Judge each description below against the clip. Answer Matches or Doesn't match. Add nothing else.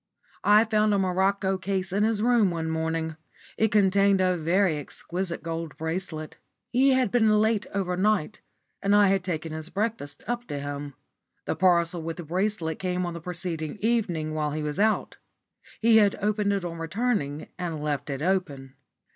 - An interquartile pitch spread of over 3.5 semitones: Matches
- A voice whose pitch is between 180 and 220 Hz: Matches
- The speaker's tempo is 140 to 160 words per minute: Doesn't match